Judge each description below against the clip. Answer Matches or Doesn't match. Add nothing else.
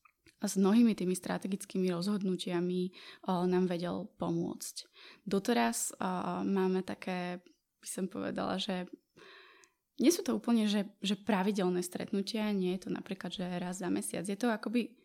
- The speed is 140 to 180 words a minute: Matches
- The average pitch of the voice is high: Matches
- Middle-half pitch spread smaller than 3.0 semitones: Doesn't match